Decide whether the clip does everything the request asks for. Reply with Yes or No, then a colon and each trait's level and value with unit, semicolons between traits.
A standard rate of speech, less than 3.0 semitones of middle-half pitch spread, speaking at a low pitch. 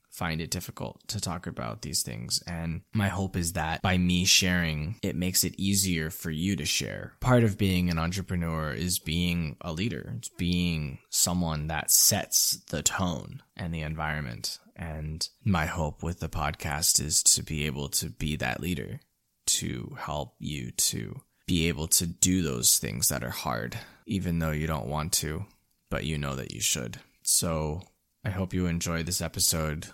Yes: average, 180 wpm; narrow, 2.6 semitones; very low, 85 Hz